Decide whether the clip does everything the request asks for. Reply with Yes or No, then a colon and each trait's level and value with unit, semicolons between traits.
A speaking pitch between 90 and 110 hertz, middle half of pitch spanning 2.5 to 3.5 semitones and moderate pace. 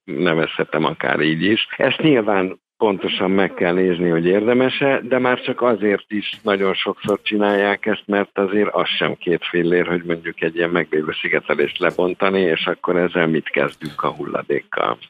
No: very low, 95 Hz; average, 2.9 semitones; fast, 160 wpm